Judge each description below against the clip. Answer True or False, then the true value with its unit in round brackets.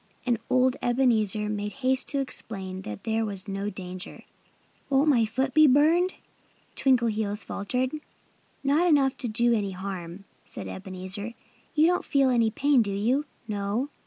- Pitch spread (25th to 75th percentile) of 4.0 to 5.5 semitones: True (5.0 semitones)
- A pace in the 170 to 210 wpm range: False (150 wpm)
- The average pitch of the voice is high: True (230 Hz)